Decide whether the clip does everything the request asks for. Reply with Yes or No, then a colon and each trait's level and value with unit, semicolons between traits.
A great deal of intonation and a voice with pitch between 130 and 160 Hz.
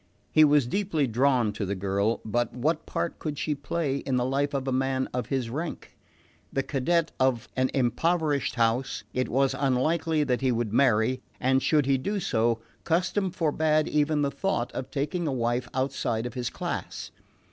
No: average, 3.7 semitones; low, 135 Hz